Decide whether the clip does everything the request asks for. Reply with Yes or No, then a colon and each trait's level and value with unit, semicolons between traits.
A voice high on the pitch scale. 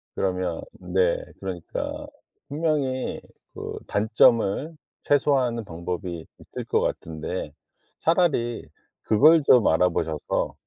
No: low, 105 Hz